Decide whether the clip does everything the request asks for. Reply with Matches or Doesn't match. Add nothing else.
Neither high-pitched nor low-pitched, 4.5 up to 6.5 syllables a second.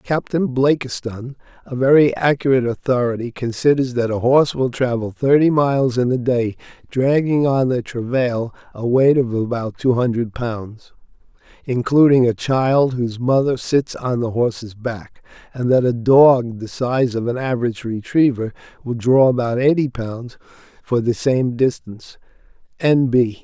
Doesn't match